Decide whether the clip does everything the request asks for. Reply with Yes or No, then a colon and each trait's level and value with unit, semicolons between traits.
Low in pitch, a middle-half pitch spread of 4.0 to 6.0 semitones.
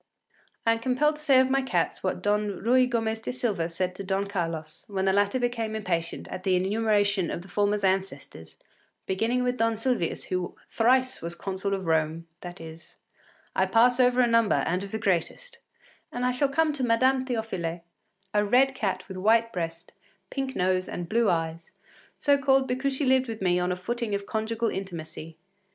No: high, 210 Hz; average, 5.3 semitones